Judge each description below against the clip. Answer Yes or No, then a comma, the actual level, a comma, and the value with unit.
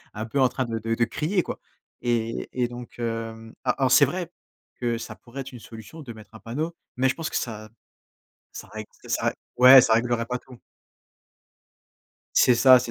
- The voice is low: Yes, low, 120 Hz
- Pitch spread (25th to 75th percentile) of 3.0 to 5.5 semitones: No, narrow, 2.6 semitones